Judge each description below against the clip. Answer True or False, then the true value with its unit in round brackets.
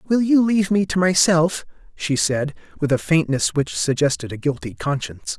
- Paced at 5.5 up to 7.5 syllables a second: False (5.2 syllables/s)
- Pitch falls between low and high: True (160 Hz)